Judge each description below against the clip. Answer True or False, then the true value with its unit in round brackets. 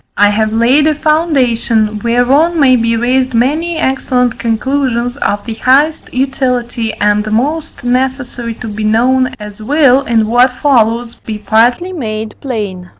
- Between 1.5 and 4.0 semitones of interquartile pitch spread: True (3.4 semitones)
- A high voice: True (245 Hz)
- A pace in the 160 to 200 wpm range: False (145 wpm)